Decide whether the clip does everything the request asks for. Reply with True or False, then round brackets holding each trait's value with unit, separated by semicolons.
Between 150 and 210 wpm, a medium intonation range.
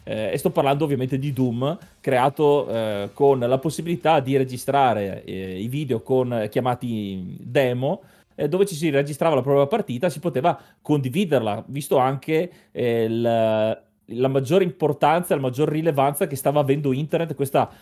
True (160 wpm; 4.3 semitones)